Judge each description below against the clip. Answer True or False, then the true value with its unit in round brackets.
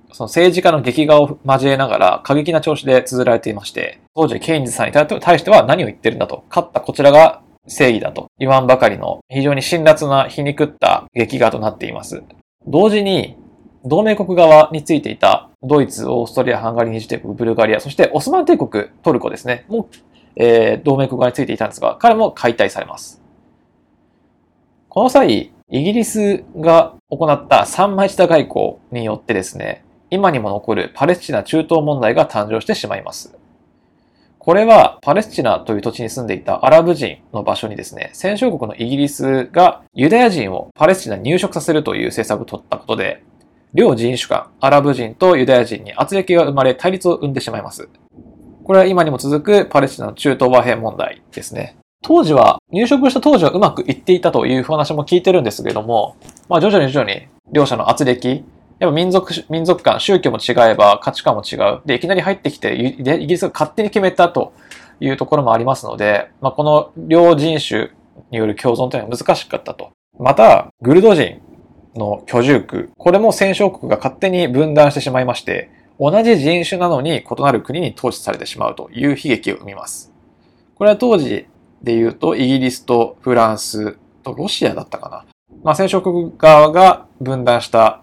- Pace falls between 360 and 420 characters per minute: True (375 characters per minute)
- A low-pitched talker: False (150 Hz)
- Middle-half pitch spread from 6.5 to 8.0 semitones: False (6.1 semitones)